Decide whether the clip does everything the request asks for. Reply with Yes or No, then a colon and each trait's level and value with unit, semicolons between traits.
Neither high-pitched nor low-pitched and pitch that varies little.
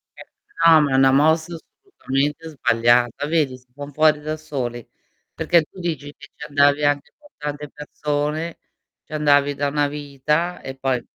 Yes: medium, 145 Hz; narrow, 2.0 semitones